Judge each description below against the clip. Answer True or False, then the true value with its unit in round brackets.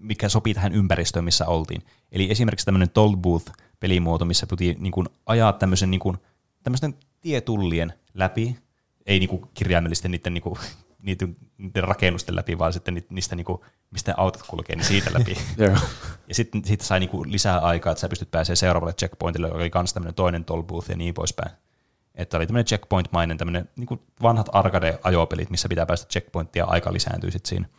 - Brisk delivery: True (165 wpm)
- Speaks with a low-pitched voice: True (95 Hz)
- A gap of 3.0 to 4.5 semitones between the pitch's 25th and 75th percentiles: True (3.4 semitones)